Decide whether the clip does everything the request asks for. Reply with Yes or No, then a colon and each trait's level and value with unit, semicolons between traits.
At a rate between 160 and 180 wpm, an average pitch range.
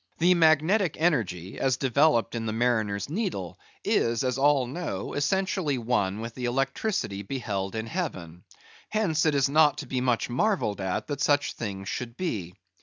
No: average, 165 wpm; wide, 6.4 semitones